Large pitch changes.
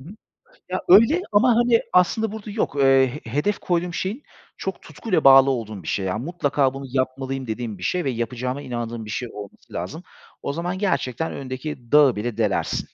Yes: wide, 7.1 semitones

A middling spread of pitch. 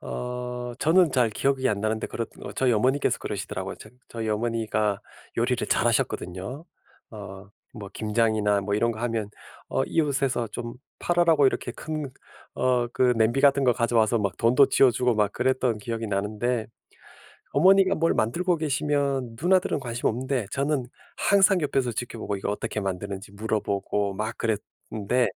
Yes: average, 4.2 semitones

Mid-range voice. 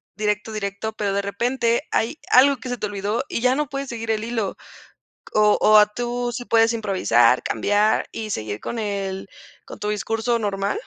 No: high, 215 Hz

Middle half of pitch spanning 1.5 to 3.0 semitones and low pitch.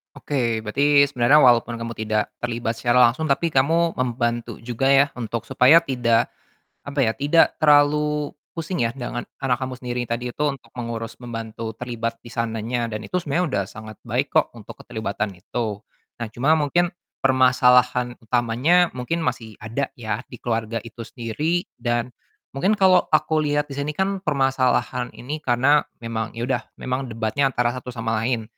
No: average, 3.6 semitones; low, 125 Hz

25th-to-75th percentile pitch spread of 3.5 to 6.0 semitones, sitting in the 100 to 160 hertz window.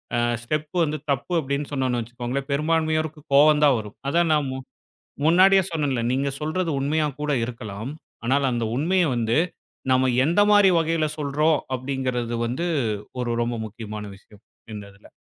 Yes: average, 4.5 semitones; medium, 140 Hz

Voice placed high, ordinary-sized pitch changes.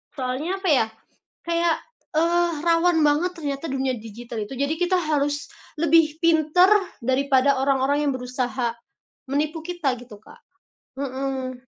Yes: very high, 285 Hz; average, 4.1 semitones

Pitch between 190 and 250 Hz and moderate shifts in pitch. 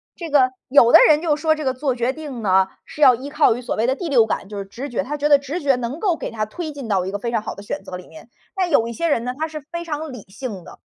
No: very high, 265 Hz; average, 4.9 semitones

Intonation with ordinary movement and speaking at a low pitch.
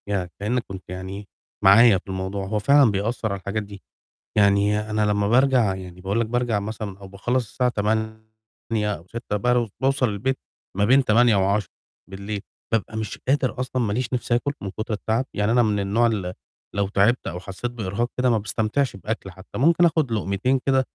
Yes: average, 3.5 semitones; low, 110 Hz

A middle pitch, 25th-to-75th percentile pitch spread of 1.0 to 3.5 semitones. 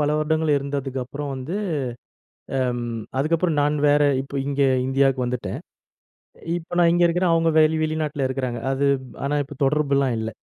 Yes: medium, 145 Hz; narrow, 2.6 semitones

